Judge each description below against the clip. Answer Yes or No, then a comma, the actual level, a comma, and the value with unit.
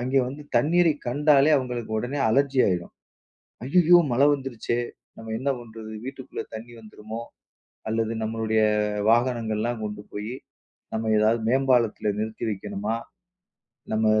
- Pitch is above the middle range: No, low, 115 Hz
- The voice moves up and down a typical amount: Yes, average, 3.5 semitones